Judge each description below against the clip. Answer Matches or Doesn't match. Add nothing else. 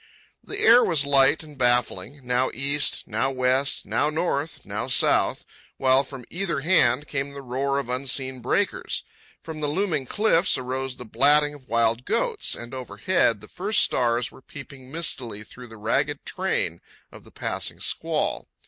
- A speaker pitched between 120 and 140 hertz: Matches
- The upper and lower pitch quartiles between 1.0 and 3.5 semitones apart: Matches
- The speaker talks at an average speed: Matches